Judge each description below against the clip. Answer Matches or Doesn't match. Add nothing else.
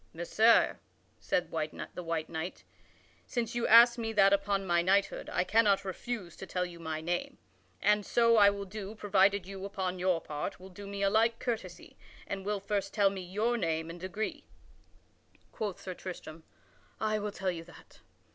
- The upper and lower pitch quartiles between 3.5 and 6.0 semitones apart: Doesn't match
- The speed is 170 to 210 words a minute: Matches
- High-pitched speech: Matches